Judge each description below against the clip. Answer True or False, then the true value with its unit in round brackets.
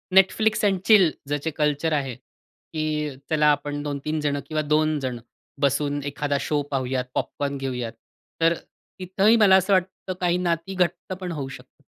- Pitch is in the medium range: True (155 Hz)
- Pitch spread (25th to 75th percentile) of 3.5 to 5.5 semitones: True (4.1 semitones)